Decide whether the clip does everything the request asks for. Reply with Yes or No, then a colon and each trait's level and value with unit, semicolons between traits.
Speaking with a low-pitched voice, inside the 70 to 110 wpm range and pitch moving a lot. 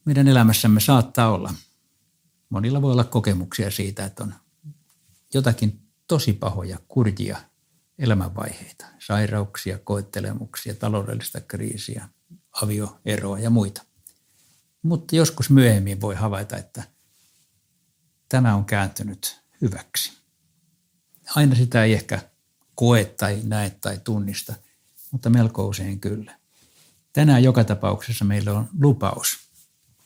No: low, 110 Hz; average, 105 wpm; average, 4.8 semitones